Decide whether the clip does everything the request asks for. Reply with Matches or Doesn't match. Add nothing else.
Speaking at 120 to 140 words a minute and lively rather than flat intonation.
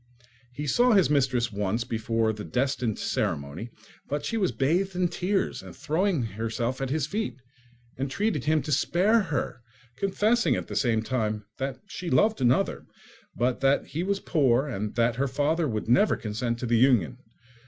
Doesn't match